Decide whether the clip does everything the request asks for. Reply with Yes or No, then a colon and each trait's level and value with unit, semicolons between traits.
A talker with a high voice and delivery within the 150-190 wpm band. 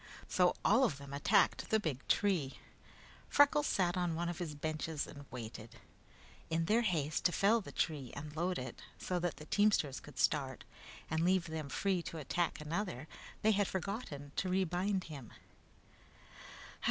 No: medium, 165 Hz; average, 165 wpm